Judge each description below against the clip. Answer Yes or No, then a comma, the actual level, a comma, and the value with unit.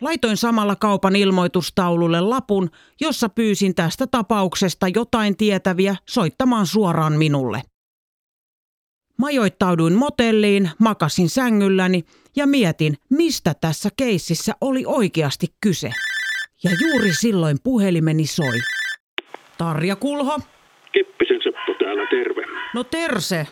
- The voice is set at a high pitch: Yes, high, 200 Hz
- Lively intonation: Yes, wide, 6.2 semitones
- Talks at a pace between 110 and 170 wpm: No, slow, 95 wpm